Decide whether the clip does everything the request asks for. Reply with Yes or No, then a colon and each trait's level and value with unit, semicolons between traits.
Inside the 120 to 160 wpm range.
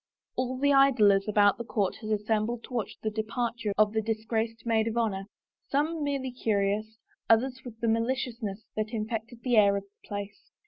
No: average, 185 wpm